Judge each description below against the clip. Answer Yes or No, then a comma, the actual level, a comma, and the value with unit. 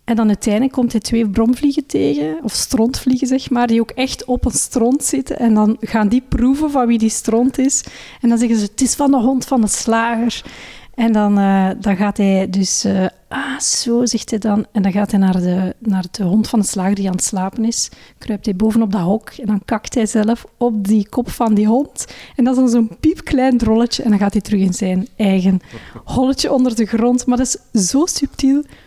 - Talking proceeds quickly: Yes, fast, 230 wpm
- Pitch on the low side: No, high, 225 Hz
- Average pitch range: Yes, average, 3.4 semitones